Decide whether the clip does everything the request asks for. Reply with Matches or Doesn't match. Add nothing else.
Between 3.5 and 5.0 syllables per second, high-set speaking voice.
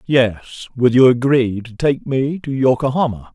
Doesn't match